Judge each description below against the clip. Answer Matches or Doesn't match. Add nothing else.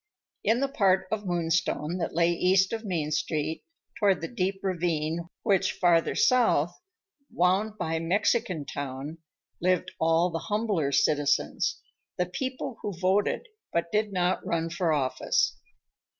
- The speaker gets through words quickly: Doesn't match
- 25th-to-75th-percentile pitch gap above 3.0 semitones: Matches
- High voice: Doesn't match